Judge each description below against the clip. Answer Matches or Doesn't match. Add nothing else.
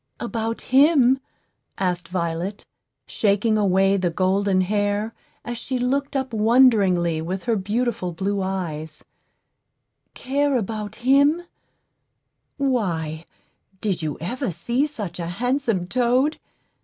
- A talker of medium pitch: Doesn't match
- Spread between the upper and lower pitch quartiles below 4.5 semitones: Doesn't match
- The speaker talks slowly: Matches